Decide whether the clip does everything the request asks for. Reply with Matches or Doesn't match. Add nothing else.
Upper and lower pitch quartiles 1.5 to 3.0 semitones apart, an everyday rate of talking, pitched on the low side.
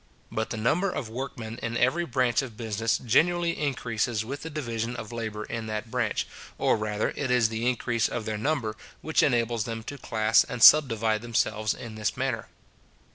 Matches